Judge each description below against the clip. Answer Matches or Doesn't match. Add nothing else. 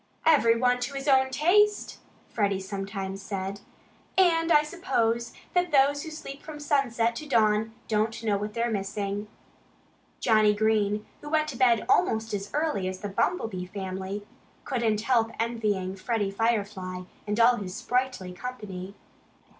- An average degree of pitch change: Matches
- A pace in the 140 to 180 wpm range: Matches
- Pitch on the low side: Doesn't match